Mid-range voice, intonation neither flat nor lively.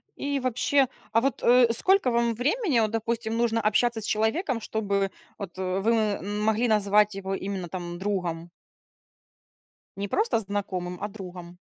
No: high, 215 Hz; average, 3.4 semitones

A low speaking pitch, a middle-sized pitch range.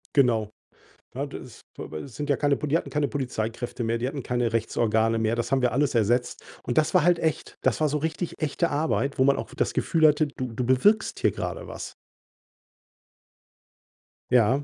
Yes: low, 130 Hz; average, 4.1 semitones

